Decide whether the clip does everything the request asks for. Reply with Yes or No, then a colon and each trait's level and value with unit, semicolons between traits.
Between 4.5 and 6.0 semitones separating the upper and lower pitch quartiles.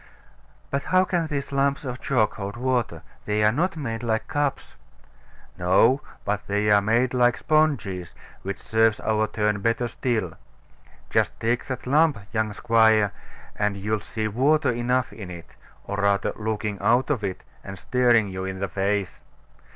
No: average, 3.9 semitones